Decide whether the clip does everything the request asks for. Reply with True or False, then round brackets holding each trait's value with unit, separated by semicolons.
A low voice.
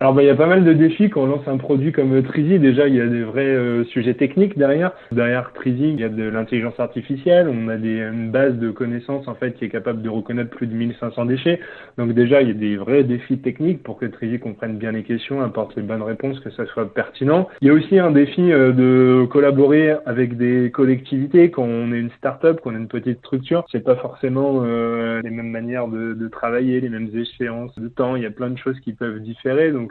True (125 Hz)